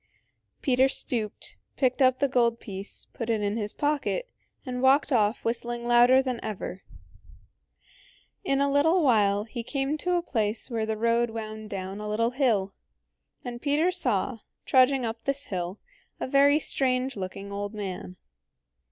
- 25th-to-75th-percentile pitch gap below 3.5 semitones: No, average, 4.2 semitones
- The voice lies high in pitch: Yes, high, 240 Hz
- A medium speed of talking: Yes, average, 155 wpm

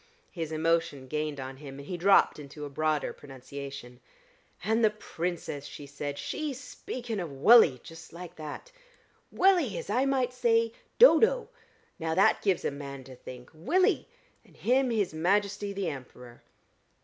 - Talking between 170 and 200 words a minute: No, average, 155 wpm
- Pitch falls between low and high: Yes, medium, 165 Hz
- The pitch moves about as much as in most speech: No, wide, 8.3 semitones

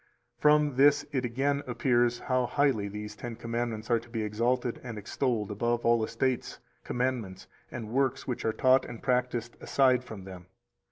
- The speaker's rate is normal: Yes, average, 170 wpm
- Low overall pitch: Yes, low, 120 Hz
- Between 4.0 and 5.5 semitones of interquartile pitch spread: No, narrow, 2.5 semitones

